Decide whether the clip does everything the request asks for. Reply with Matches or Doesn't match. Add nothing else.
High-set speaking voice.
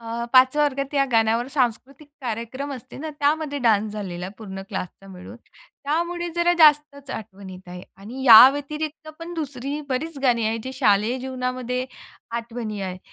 Matches